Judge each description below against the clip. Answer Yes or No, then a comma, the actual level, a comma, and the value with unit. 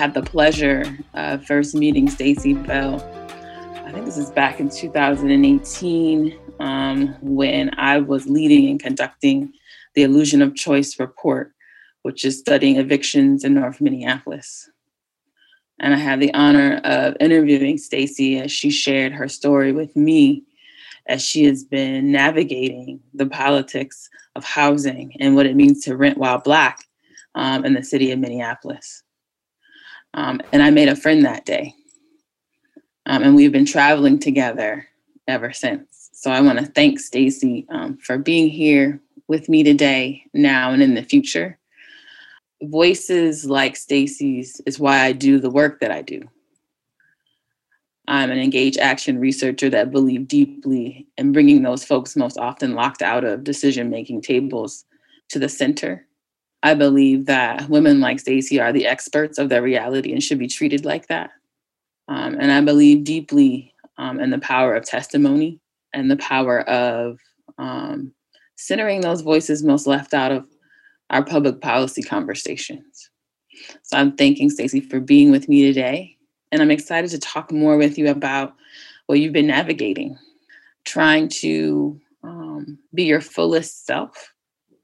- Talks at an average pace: Yes, average, 150 wpm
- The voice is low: No, medium, 155 Hz